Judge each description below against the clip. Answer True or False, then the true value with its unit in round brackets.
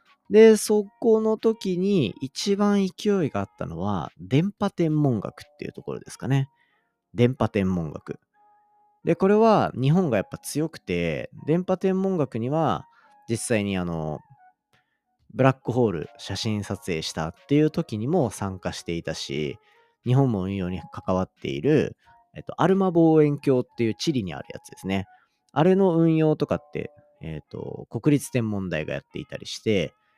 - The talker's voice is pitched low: False (145 Hz)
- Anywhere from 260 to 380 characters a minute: True (300 characters per minute)